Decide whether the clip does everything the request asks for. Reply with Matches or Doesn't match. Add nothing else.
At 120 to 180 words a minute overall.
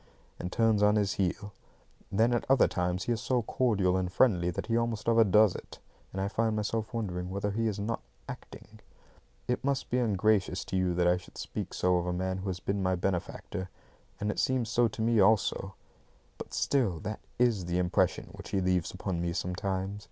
Doesn't match